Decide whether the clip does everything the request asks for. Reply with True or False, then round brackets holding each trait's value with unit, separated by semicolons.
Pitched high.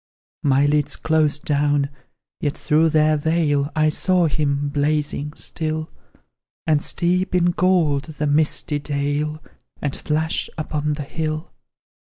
False (150 Hz)